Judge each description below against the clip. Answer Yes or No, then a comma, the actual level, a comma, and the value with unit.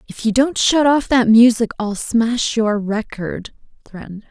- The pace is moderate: Yes, average, 180 wpm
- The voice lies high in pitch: Yes, high, 230 Hz